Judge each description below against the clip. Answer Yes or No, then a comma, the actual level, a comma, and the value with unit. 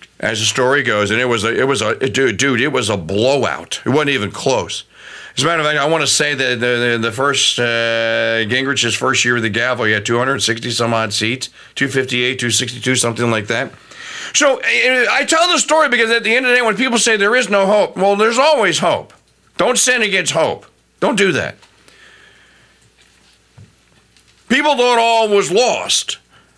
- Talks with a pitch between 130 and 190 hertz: Yes, medium, 140 Hz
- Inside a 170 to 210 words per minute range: Yes, average, 200 wpm